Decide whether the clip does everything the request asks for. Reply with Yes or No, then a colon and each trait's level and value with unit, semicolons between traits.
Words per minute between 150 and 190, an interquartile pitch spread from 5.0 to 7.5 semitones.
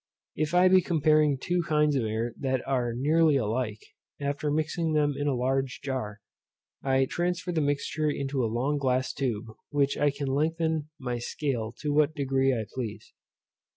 No: average, 175 wpm; average, 3.1 semitones